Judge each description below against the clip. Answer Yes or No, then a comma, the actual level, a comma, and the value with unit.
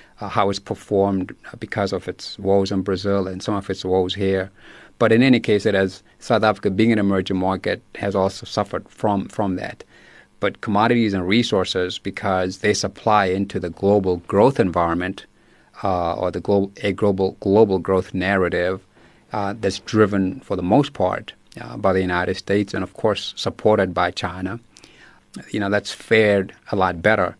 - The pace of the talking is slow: No, average, 175 wpm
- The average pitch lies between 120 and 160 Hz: No, very low, 95 Hz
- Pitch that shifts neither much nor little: No, narrow, 1.8 semitones